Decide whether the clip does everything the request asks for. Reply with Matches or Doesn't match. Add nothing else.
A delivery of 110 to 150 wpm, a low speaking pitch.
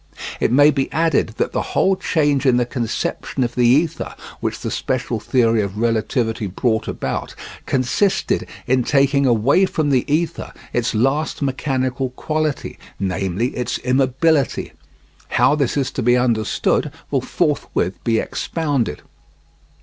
Matches